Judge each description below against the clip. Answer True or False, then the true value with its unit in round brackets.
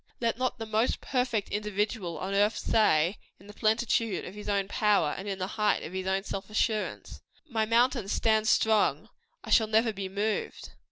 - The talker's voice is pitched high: True (210 Hz)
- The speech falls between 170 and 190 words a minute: True (180 wpm)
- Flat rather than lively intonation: True (2.2 semitones)